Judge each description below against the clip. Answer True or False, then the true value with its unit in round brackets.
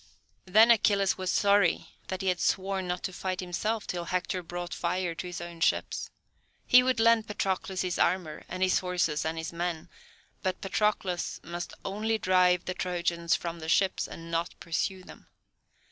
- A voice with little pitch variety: True (1.9 semitones)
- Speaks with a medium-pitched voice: True (180 Hz)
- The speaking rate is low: False (175 wpm)